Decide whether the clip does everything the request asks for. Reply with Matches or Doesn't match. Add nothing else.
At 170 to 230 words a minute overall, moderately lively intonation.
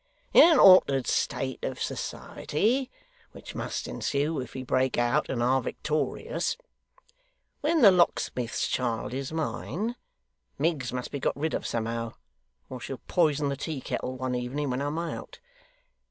Doesn't match